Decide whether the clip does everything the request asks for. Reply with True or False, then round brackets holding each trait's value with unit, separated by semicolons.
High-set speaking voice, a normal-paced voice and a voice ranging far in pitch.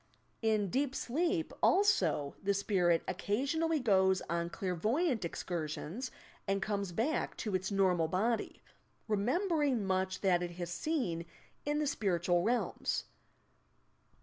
False (200 Hz; 120 wpm; 6.7 semitones)